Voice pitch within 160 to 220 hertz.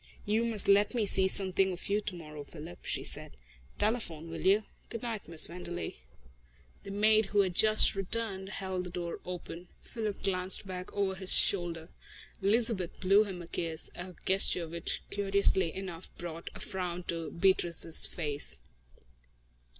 Yes: high, 190 Hz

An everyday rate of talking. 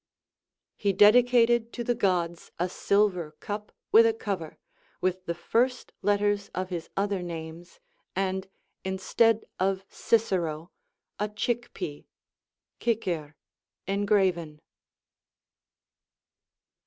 No: slow, 100 wpm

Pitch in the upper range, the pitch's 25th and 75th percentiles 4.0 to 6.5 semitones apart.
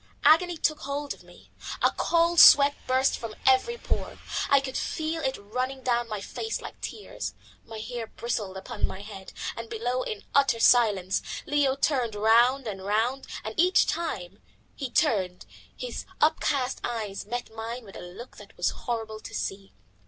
Yes: high, 245 Hz; average, 4.5 semitones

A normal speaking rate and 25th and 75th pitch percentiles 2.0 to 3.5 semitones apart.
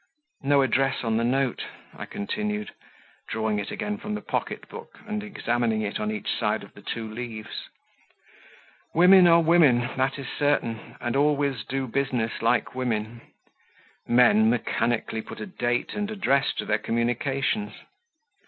No: average, 150 wpm; average, 4.5 semitones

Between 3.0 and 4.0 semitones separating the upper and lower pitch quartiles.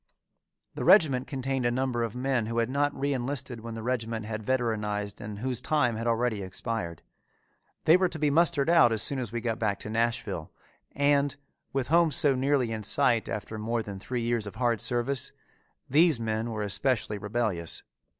Yes: average, 3.6 semitones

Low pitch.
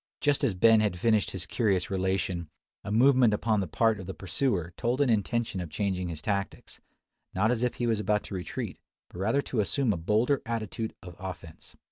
Yes: low, 105 Hz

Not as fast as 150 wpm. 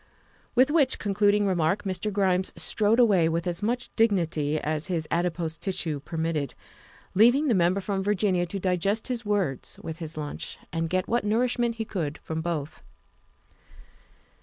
No: average, 160 wpm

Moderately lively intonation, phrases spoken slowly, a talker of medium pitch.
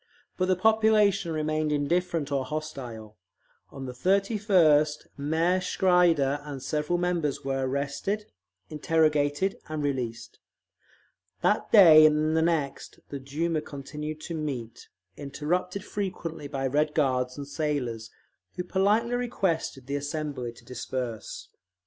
Yes: average, 4.3 semitones; slow, 120 wpm; medium, 150 Hz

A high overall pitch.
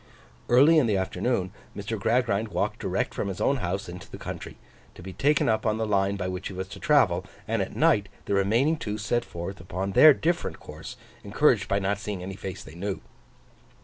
No: low, 100 Hz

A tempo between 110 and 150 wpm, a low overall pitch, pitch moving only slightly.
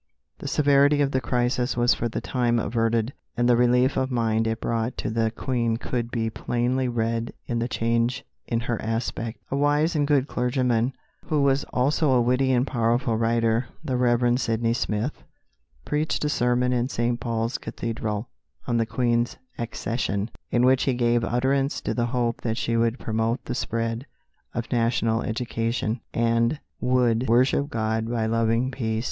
No: average, 170 wpm; low, 120 Hz; narrow, 1.9 semitones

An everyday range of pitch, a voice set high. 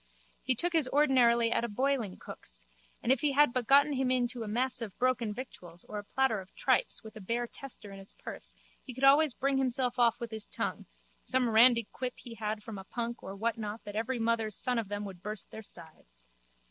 Yes: average, 3.4 semitones; high, 235 Hz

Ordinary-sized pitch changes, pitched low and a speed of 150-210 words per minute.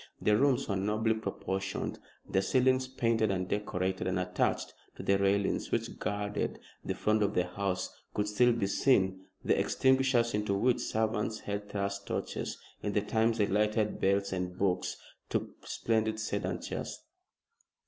No: narrow, 2.3 semitones; low, 105 Hz; average, 155 wpm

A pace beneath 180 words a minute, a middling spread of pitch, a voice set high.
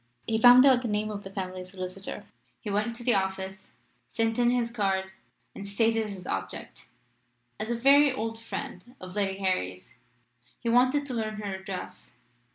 Yes: average, 170 wpm; average, 3.8 semitones; high, 215 Hz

